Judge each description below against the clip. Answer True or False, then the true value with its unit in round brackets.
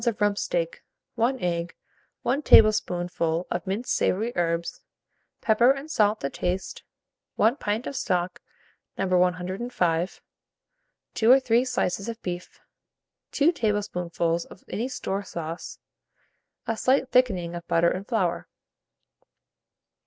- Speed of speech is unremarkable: False (125 wpm)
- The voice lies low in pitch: False (195 Hz)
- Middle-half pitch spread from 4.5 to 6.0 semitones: True (5.1 semitones)